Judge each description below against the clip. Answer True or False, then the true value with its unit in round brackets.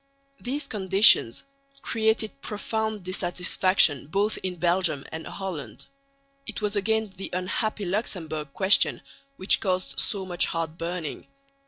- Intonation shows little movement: False (3.6 semitones)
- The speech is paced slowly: True (120 wpm)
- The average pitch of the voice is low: False (190 Hz)